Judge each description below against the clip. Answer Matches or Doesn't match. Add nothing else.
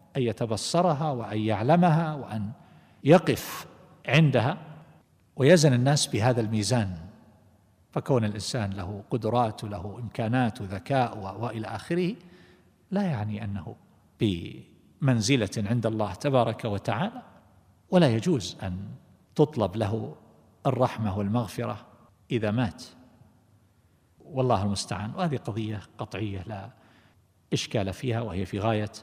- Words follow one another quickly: Doesn't match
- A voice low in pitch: Matches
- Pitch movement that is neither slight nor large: Matches